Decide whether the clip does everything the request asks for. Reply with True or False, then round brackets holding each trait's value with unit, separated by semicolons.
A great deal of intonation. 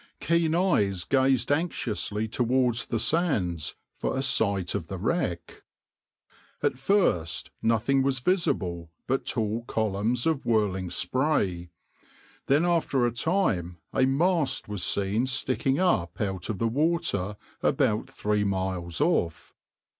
True (6.1 semitones)